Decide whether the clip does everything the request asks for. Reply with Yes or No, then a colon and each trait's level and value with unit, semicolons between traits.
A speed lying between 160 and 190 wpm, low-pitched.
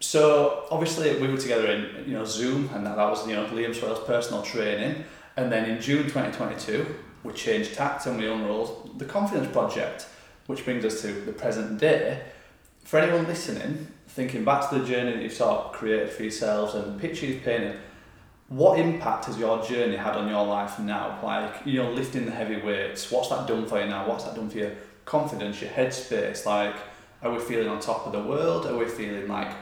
No: fast, 205 wpm; low, 115 Hz